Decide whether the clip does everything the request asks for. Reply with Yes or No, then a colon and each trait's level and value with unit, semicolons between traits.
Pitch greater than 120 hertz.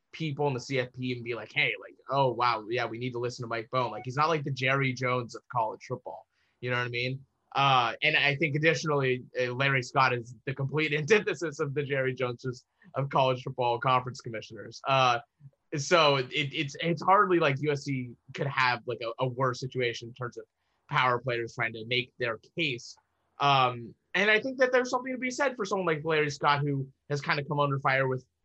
Yes: low, 135 Hz